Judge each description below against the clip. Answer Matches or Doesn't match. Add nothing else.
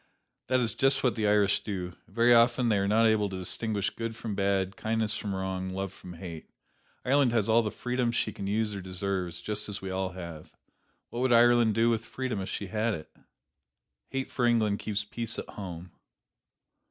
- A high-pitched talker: Doesn't match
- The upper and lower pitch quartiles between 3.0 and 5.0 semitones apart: Matches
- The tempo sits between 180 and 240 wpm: Matches